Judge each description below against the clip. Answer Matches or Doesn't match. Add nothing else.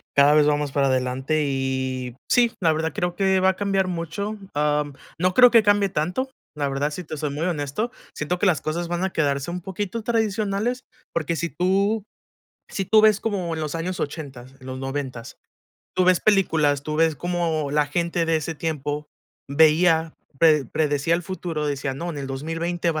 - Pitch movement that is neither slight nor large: Matches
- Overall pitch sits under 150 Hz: Doesn't match